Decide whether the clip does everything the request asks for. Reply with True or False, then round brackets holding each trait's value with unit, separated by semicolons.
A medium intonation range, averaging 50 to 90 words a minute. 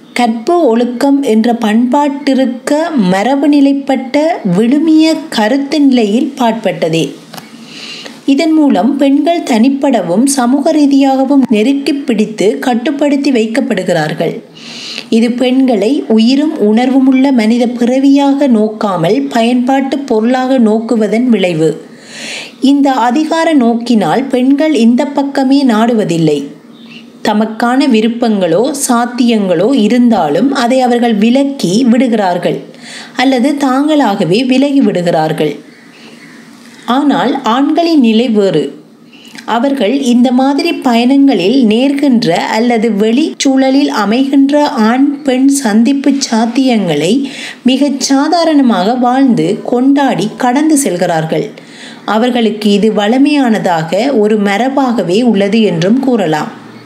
True (3.4 semitones; 85 wpm)